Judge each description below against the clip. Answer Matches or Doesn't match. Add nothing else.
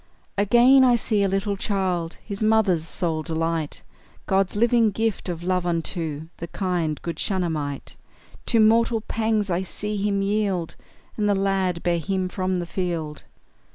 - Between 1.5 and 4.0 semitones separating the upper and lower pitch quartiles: Matches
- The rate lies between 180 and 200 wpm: Doesn't match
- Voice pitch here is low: Doesn't match